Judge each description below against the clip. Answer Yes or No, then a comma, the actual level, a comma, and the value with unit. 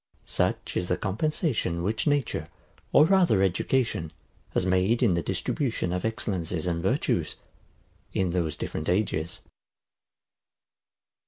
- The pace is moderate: No, slow, 115 wpm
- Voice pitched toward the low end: Yes, very low, 95 Hz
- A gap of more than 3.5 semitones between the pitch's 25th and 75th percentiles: Yes, average, 5.1 semitones